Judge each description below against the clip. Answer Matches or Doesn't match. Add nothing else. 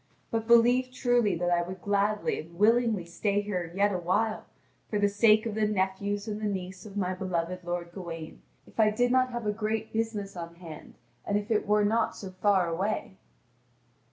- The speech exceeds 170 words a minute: Matches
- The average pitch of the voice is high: Matches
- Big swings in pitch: Doesn't match